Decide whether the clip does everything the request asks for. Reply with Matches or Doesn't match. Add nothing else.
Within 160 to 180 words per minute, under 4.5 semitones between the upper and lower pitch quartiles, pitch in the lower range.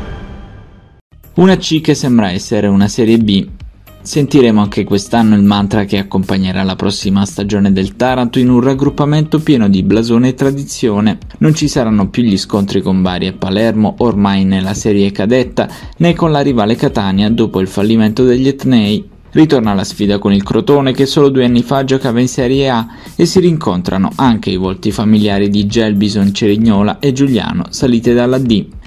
Doesn't match